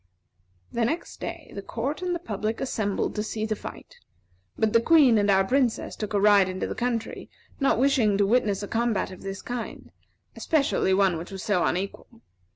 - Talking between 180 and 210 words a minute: Yes, average, 190 wpm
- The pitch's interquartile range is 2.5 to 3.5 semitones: No, average, 3.9 semitones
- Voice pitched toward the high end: Yes, high, 220 Hz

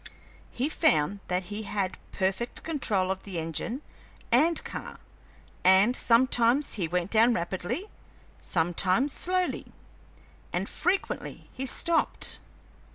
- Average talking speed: No, slow, 110 wpm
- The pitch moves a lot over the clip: Yes, wide, 6.0 semitones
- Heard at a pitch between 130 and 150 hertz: No, high, 210 Hz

